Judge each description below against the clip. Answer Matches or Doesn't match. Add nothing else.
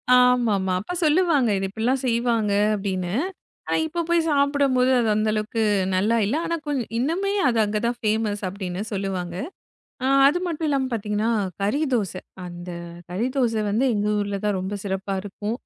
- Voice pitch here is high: Matches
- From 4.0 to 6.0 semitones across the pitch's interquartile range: Matches